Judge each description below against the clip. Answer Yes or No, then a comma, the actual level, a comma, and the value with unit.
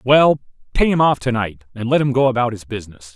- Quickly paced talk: Yes, fast, 245 wpm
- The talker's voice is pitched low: Yes, low, 120 Hz